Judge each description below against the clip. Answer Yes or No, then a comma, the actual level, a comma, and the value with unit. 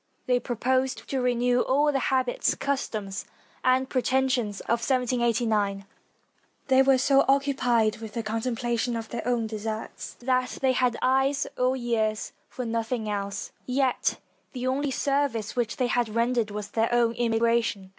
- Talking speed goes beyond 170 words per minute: No, average, 150 wpm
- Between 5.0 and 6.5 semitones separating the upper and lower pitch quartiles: No, narrow, 2.6 semitones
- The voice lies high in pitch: Yes, high, 240 Hz